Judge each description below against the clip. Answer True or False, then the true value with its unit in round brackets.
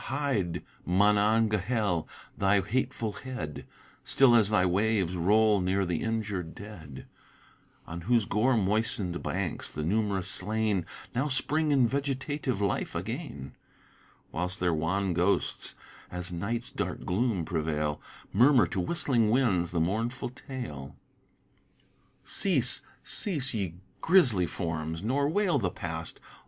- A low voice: True (105 Hz)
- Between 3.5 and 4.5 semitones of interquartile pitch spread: False (5.6 semitones)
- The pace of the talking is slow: True (120 wpm)